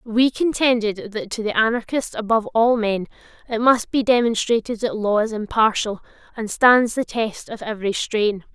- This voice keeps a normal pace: Yes, average, 170 wpm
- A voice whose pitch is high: Yes, high, 225 Hz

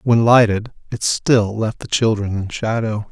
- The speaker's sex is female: No, male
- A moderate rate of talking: Yes, average, 175 wpm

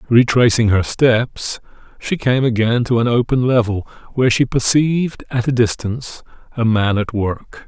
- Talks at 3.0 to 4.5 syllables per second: No, 4.7 syllables/s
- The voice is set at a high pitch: No, low, 120 Hz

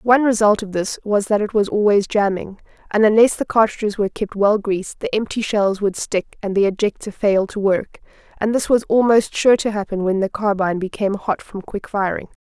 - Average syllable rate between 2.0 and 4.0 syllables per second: No, 5.5 syllables/s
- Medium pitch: No, high, 205 Hz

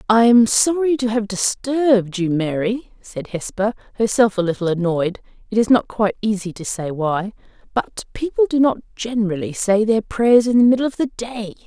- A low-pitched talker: No, high, 215 Hz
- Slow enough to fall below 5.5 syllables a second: Yes, 5.1 syllables/s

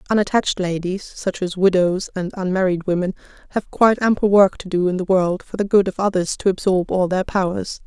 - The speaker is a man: No, female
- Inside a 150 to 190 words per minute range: No, fast, 205 wpm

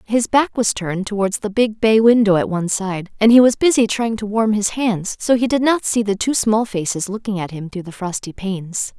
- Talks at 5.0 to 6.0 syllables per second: Yes, 5.3 syllables/s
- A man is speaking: No, female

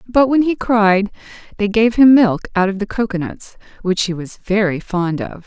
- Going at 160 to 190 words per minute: No, average, 200 wpm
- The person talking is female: Yes, female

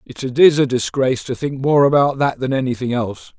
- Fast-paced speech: Yes, fast, 215 wpm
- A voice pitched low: Yes, low, 130 Hz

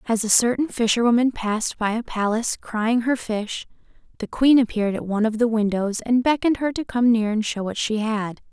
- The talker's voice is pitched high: Yes, high, 230 Hz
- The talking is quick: Yes, fast, 210 wpm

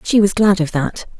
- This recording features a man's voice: No, female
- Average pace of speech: No, fast, 250 wpm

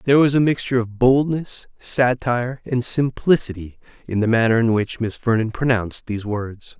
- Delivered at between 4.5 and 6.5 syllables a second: Yes, 5.3 syllables/s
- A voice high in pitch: No, low, 120 Hz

